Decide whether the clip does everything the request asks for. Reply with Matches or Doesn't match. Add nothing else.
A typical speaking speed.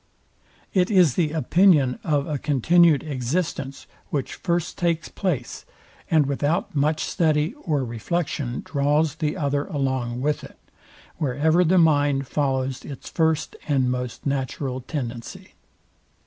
Doesn't match